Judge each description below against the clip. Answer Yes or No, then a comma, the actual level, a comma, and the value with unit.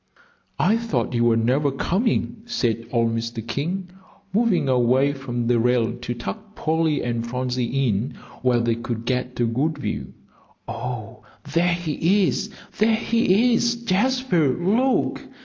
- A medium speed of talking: Yes, average, 145 wpm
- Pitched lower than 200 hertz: Yes, low, 135 Hz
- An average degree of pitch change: No, wide, 8.4 semitones